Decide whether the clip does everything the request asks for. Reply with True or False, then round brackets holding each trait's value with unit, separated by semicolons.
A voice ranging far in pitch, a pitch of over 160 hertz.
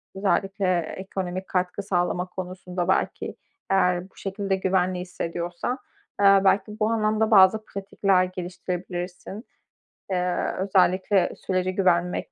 False (1.6 semitones; 185 Hz)